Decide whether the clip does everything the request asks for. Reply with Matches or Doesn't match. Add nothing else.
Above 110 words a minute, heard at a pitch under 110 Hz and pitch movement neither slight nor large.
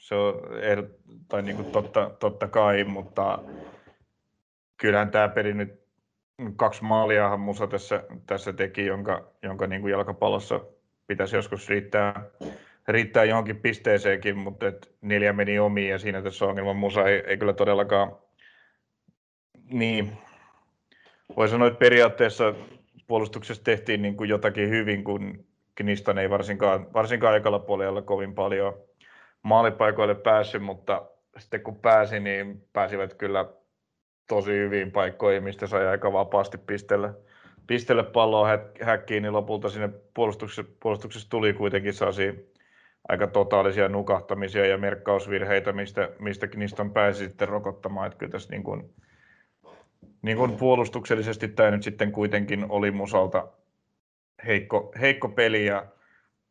Doesn't match